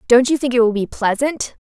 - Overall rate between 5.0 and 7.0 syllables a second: Yes, 5.6 syllables/s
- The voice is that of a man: No, female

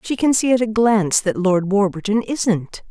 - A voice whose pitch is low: No, high, 210 Hz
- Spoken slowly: No, fast, 205 wpm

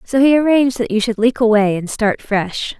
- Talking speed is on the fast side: Yes, fast, 235 wpm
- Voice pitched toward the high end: Yes, high, 235 Hz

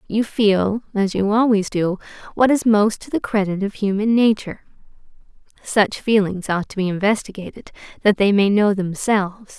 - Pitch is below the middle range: No, high, 205 Hz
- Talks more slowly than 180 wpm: Yes, average, 165 wpm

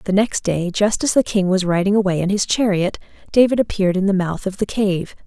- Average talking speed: No, fast, 240 wpm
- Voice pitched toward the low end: No, high, 195 Hz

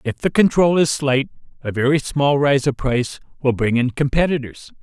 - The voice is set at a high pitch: No, low, 135 Hz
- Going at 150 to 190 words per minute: Yes, average, 185 wpm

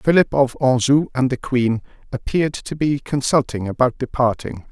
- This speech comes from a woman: No, male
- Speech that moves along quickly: No, average, 155 wpm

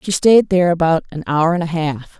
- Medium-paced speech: No, fast, 245 wpm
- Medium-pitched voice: Yes, medium, 170 Hz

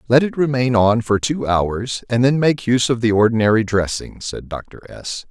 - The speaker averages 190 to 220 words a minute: Yes, fast, 205 wpm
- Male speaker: Yes, male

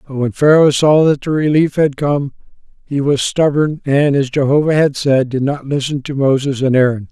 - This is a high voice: No, medium, 140 Hz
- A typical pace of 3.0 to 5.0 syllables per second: Yes, 4.8 syllables/s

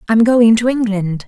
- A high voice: Yes, high, 220 Hz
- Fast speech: No, average, 190 wpm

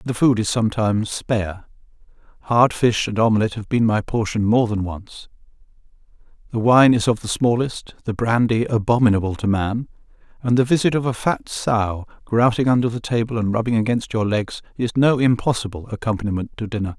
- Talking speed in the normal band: Yes, average, 175 wpm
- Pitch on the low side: Yes, low, 115 Hz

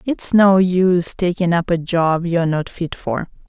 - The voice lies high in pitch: No, medium, 175 Hz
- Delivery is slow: No, fast, 205 wpm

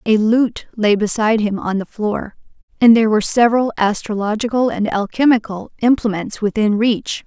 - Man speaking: No, female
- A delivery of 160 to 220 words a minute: No, average, 150 wpm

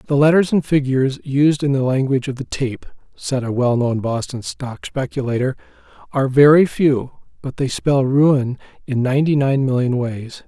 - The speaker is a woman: No, male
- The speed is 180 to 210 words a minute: No, average, 165 wpm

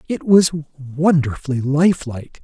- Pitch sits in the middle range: Yes, medium, 150 Hz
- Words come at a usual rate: No, slow, 125 wpm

